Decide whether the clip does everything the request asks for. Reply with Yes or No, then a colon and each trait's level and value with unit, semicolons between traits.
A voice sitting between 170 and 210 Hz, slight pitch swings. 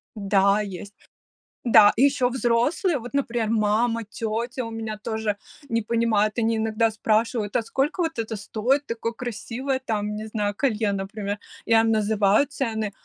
No: high, 225 Hz; narrow, 2.2 semitones